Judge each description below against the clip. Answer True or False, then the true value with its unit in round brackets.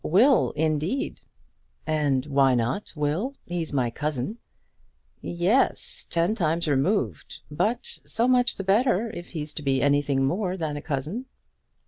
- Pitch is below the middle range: False (160 Hz)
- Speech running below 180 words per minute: True (135 wpm)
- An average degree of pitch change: False (6.2 semitones)